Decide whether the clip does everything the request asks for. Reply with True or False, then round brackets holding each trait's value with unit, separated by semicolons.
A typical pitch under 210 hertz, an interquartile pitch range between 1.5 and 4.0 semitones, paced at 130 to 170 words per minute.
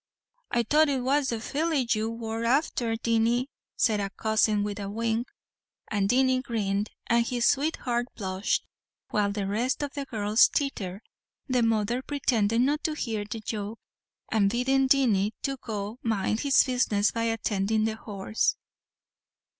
False (230 Hz; 3.5 semitones; 155 wpm)